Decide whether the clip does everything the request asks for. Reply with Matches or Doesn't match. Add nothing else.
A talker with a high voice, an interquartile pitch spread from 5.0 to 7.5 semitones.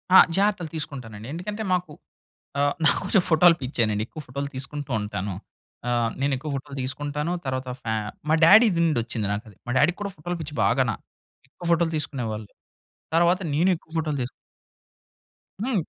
Doesn't match